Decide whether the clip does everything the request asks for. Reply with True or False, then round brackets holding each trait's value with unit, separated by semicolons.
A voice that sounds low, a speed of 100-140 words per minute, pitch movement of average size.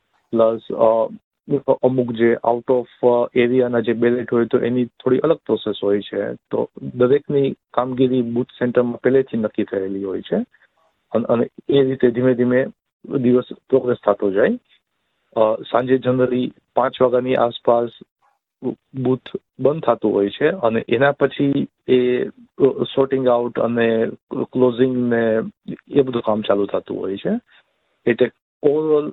False (125 Hz; 130 wpm; 1.9 semitones)